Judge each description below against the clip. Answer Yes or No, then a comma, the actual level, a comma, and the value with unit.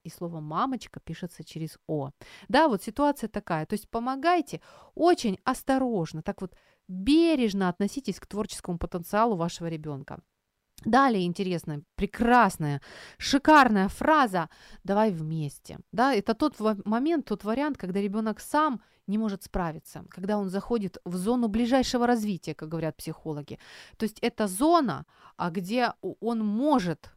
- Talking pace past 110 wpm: Yes, average, 135 wpm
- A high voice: Yes, high, 205 Hz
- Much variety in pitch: Yes, wide, 5.8 semitones